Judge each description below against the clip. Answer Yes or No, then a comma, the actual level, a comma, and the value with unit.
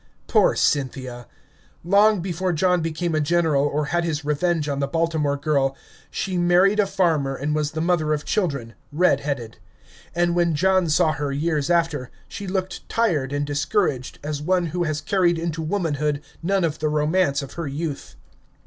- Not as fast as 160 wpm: No, average, 175 wpm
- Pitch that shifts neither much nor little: Yes, average, 3.4 semitones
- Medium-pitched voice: Yes, medium, 155 Hz